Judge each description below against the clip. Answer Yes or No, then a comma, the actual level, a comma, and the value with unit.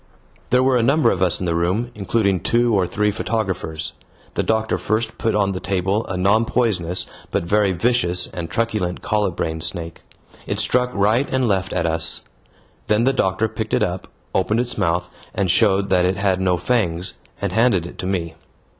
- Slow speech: No, average, 190 wpm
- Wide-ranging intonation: No, average, 4.0 semitones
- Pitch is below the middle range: Yes, low, 100 Hz